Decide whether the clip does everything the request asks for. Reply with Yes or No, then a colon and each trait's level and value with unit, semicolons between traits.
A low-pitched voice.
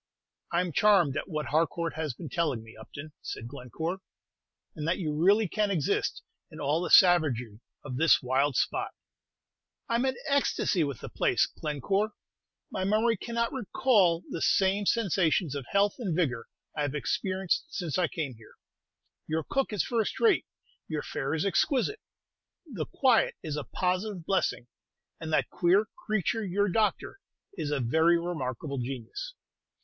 No: medium, 170 Hz